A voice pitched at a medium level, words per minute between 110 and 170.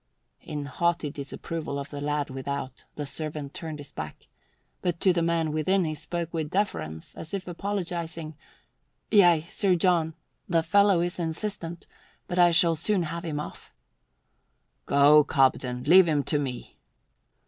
Yes: medium, 160 Hz; average, 150 wpm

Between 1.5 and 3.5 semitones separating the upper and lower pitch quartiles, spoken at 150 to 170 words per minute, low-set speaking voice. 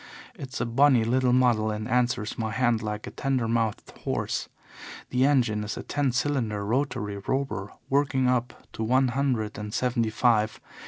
Yes: average, 3.2 semitones; average, 165 wpm; low, 120 Hz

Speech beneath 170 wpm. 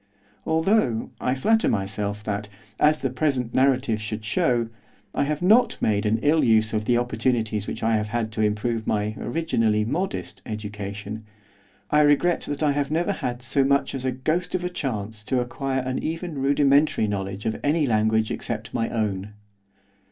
No: average, 175 wpm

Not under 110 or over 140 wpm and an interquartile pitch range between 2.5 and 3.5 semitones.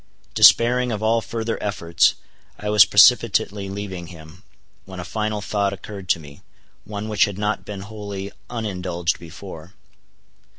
Yes: slow, 135 wpm; average, 2.9 semitones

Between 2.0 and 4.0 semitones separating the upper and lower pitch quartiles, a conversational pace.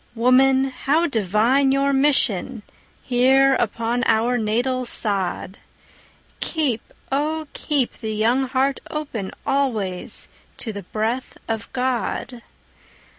No: average, 3.5 semitones; slow, 105 wpm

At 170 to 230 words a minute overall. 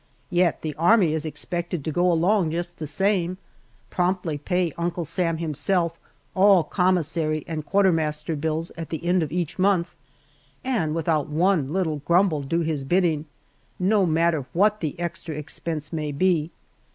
No: average, 150 wpm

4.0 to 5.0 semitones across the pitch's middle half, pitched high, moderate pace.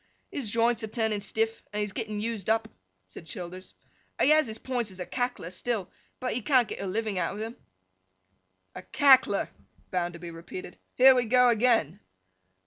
Yes: average, 4.5 semitones; high, 220 Hz; average, 180 wpm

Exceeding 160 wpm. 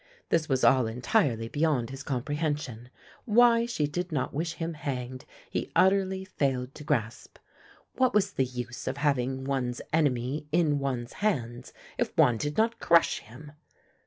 No: average, 155 wpm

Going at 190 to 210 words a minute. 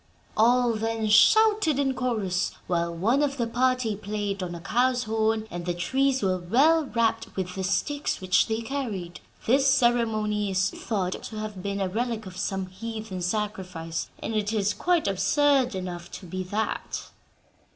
No: average, 165 wpm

